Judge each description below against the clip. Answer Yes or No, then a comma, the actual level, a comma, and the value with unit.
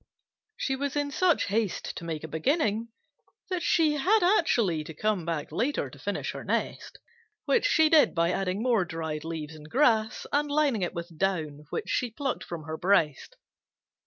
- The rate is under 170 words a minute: No, average, 180 wpm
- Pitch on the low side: No, high, 210 Hz